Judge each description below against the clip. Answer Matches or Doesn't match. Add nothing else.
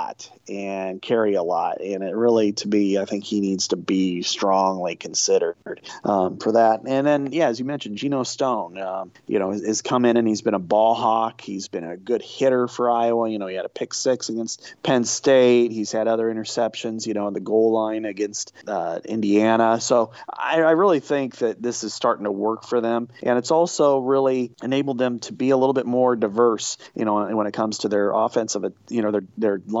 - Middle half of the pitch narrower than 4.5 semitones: Matches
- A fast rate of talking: Matches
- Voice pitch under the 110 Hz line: Doesn't match